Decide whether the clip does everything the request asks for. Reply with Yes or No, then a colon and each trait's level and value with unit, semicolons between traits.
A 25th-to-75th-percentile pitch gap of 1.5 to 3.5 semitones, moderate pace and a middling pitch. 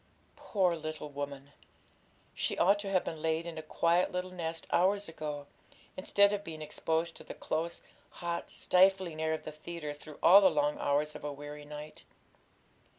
Yes: average, 3.2 semitones; average, 175 wpm; medium, 160 Hz